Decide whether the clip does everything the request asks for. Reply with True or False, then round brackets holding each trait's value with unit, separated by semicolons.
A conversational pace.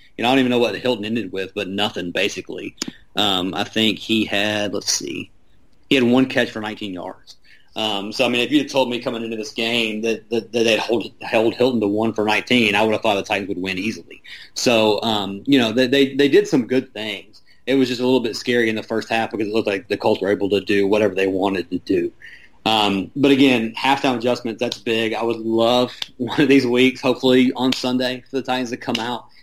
False (245 wpm)